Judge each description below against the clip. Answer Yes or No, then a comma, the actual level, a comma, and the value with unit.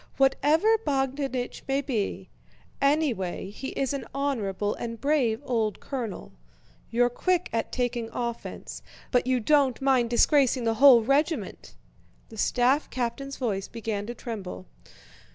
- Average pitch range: Yes, average, 3.4 semitones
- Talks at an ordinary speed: No, slow, 130 wpm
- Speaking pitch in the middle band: No, very high, 250 Hz